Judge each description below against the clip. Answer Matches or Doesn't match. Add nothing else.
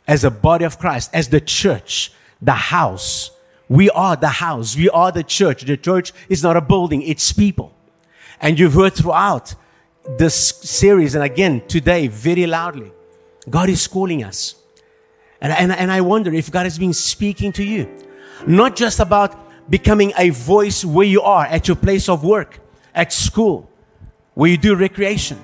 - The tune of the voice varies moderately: Matches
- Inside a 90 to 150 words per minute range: Doesn't match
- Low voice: Doesn't match